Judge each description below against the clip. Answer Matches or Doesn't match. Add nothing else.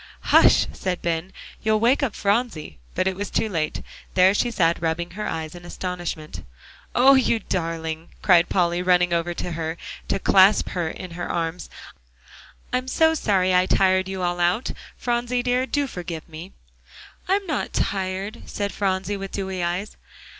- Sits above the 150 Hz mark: Matches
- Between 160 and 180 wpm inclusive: Matches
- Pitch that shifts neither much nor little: Matches